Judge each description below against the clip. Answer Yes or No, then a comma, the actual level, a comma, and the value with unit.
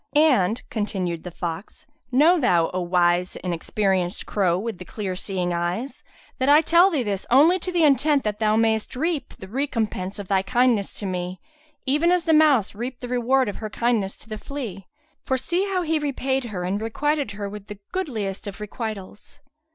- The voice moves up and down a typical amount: No, wide, 6.4 semitones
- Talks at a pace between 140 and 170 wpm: No, average, 190 wpm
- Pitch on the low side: No, high, 220 Hz